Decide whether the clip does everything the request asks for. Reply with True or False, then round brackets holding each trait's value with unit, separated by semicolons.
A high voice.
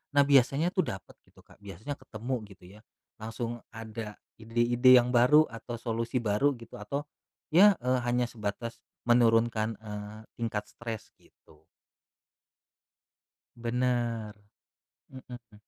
False (115 Hz)